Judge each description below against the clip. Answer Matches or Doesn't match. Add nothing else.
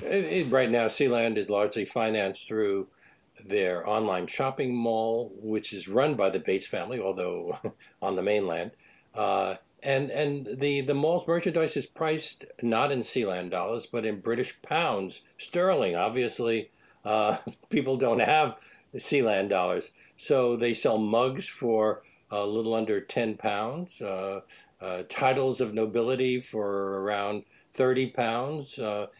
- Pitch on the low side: Matches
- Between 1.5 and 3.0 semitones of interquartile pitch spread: Doesn't match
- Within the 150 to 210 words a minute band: Doesn't match